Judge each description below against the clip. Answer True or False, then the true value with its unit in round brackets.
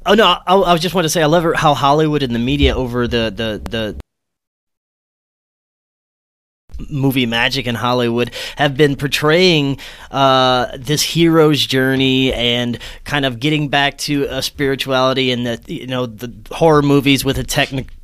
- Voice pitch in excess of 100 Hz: True (135 Hz)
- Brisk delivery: False (165 wpm)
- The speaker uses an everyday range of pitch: True (3.5 semitones)